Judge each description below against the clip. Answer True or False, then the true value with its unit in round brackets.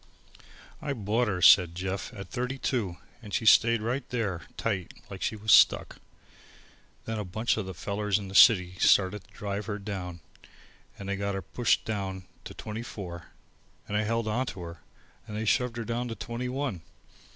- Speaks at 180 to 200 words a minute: True (190 wpm)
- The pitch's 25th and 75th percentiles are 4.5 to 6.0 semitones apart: False (3.4 semitones)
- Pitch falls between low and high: False (105 Hz)